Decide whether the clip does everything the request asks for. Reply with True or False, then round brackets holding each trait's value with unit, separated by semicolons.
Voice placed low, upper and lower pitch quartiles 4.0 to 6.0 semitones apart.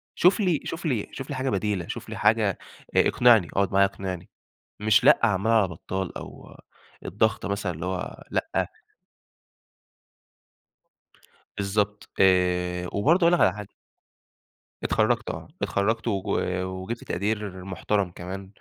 False (100 Hz; 3.3 semitones)